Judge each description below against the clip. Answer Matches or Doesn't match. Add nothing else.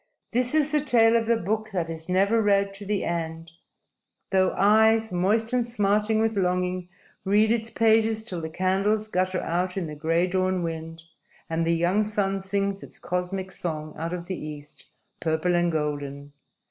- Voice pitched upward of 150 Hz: Matches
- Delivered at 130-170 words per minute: Doesn't match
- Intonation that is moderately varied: Matches